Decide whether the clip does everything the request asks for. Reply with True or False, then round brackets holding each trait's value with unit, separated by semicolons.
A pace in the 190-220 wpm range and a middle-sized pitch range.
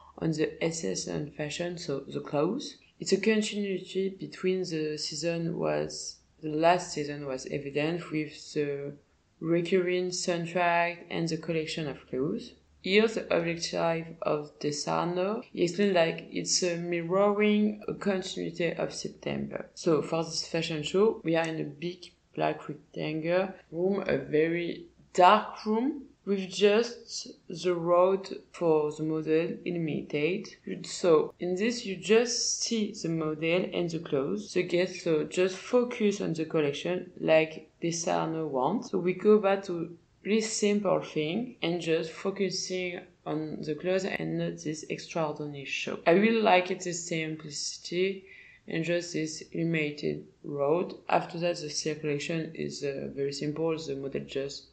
False (145 wpm; 3.6 semitones)